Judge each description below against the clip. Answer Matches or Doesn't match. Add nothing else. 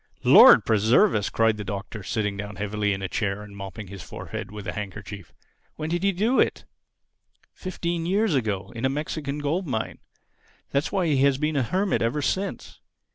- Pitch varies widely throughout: Matches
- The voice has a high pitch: Doesn't match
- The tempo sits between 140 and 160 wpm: Doesn't match